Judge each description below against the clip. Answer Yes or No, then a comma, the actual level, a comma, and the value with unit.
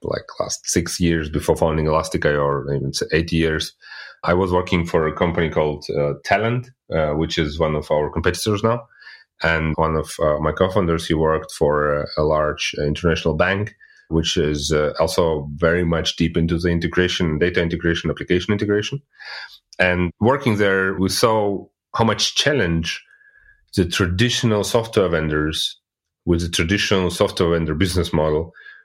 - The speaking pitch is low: Yes, very low, 85 Hz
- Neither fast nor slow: Yes, average, 160 wpm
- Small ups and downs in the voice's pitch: No, average, 3.6 semitones